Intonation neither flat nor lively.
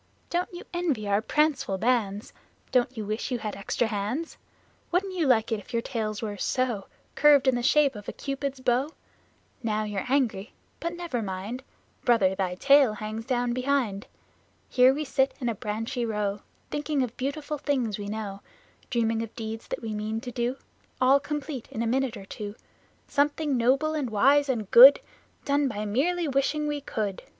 Yes: average, 4.7 semitones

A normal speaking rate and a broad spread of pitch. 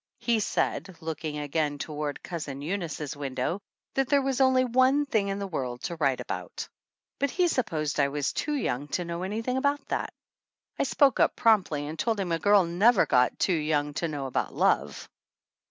Yes: average, 185 wpm; wide, 7.9 semitones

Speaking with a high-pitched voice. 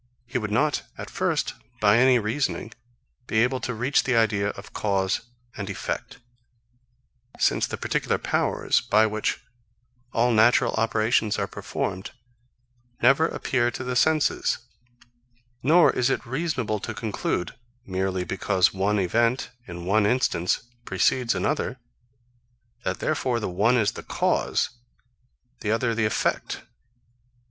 No: low, 110 Hz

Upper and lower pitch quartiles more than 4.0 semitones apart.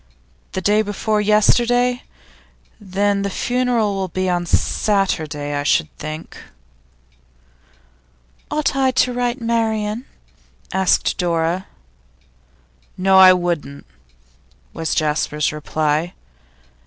Yes: average, 5.2 semitones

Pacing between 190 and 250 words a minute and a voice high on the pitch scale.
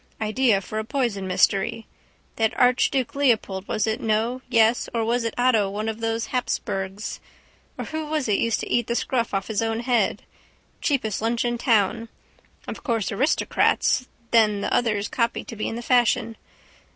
No: average, 175 wpm; high, 230 Hz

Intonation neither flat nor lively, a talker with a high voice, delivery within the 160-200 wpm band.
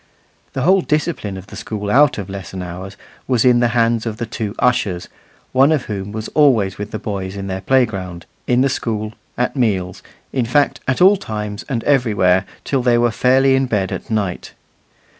No: average, 4.7 semitones; low, 110 Hz; average, 195 wpm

